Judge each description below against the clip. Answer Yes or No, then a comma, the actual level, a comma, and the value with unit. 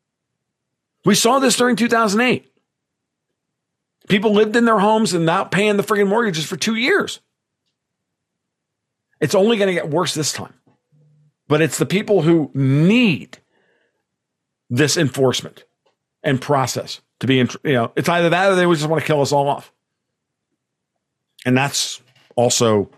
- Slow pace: No, average, 145 wpm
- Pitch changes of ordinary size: No, wide, 6.5 semitones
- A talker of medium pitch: Yes, medium, 165 Hz